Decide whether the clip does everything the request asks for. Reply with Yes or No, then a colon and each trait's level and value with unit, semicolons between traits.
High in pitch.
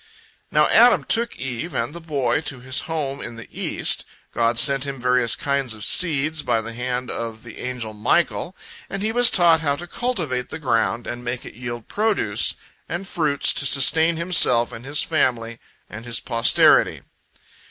No: low, 130 Hz